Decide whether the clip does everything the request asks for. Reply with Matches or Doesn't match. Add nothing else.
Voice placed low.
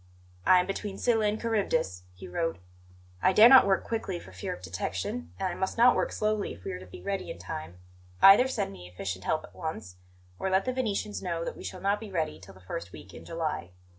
Doesn't match